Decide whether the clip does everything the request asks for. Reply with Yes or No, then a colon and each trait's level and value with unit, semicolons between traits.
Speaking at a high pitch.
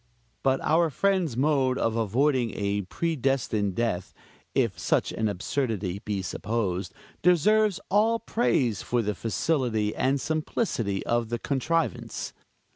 No: low, 125 Hz